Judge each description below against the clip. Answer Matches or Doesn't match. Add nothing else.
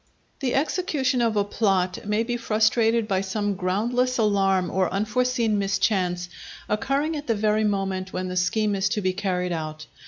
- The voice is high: Matches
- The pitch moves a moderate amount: Matches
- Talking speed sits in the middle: Matches